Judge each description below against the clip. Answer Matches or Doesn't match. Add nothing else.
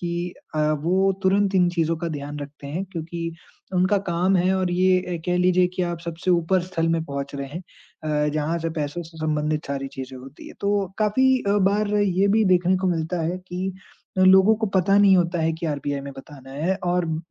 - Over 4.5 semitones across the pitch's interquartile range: Doesn't match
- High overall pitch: Doesn't match